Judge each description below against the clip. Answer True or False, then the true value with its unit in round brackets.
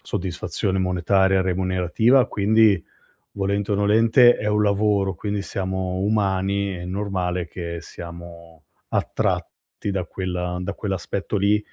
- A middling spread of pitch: False (2.2 semitones)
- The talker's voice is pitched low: True (95 Hz)